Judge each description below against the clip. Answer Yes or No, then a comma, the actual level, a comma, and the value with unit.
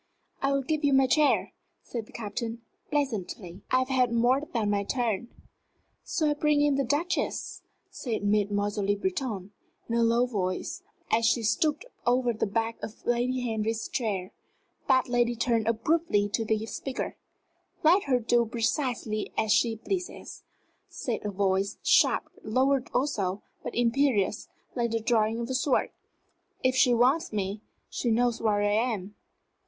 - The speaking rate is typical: Yes, average, 160 wpm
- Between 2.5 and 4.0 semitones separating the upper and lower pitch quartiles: Yes, average, 3.5 semitones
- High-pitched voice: Yes, high, 235 Hz